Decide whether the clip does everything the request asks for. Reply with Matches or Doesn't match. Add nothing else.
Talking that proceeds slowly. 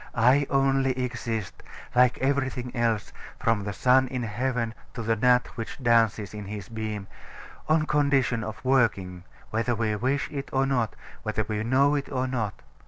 Doesn't match